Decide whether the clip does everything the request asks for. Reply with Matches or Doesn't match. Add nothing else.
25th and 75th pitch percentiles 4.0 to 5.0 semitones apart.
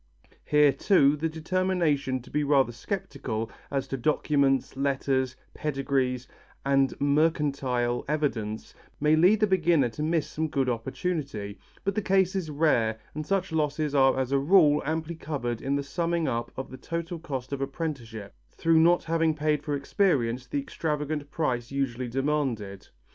Doesn't match